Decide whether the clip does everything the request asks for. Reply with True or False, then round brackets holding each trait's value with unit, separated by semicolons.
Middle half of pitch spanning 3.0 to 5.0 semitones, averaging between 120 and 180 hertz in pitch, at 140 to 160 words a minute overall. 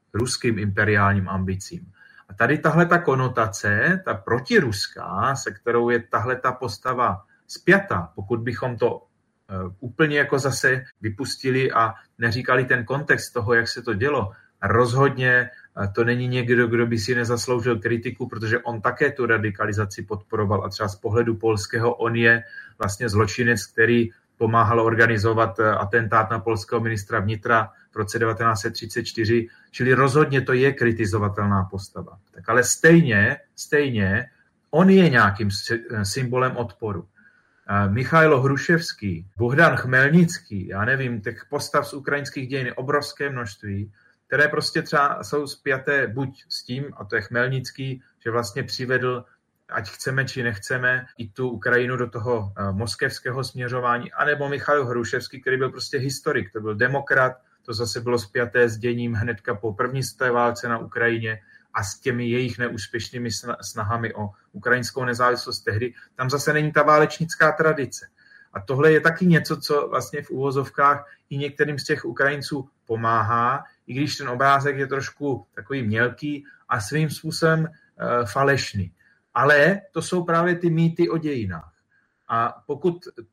True (3.6 semitones; 125 Hz; 145 wpm)